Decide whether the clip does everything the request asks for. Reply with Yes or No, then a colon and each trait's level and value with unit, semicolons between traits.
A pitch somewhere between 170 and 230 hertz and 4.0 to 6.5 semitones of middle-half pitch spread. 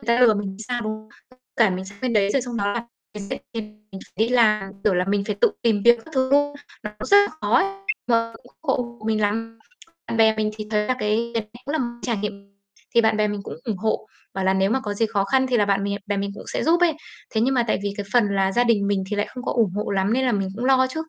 No: high, 220 Hz; average, 3.0 semitones